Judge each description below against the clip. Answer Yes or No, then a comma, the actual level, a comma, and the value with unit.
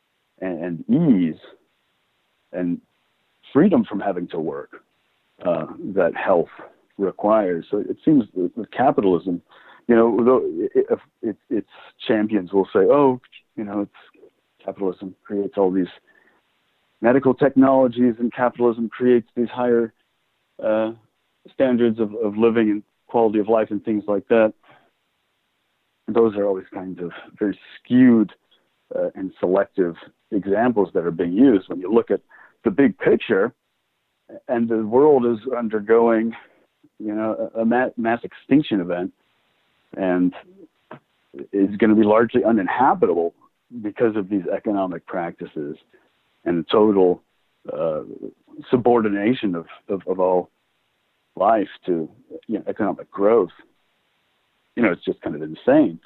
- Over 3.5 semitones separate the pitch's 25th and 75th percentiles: No, average, 3.0 semitones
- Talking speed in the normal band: No, slow, 130 wpm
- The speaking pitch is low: Yes, low, 110 Hz